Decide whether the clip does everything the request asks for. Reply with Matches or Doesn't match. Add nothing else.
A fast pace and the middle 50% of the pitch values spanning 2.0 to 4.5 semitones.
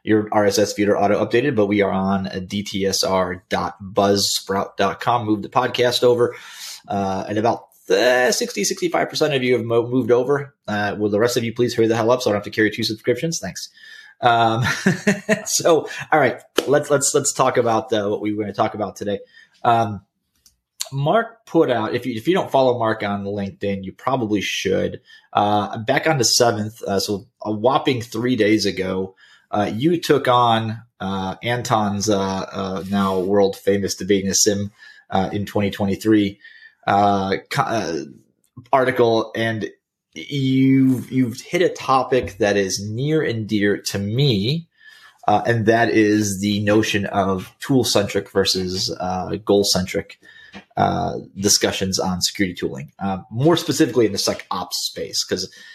Doesn't match